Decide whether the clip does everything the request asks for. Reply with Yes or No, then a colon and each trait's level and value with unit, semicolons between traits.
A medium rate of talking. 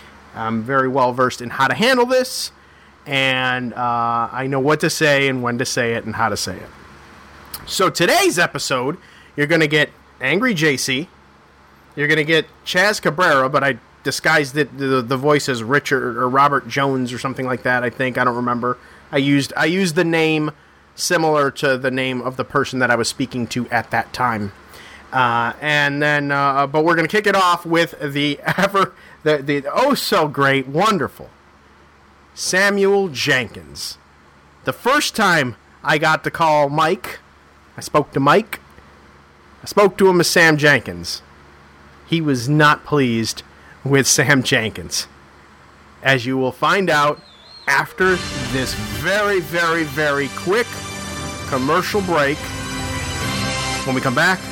Yes: average, 165 wpm